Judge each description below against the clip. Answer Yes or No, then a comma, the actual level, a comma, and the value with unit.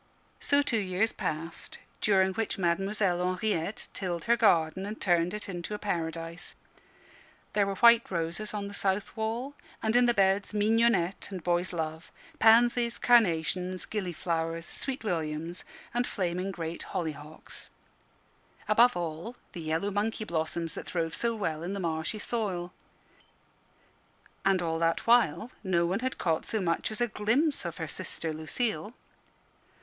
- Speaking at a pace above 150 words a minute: No, average, 145 wpm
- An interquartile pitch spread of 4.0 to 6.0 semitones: Yes, average, 4.6 semitones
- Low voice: No, high, 190 Hz